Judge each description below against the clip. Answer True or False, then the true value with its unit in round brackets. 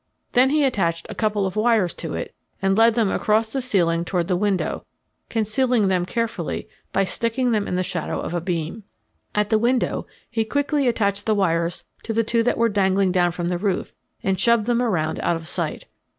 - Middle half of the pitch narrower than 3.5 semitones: False (4.4 semitones)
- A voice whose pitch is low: False (205 Hz)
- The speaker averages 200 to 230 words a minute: True (205 wpm)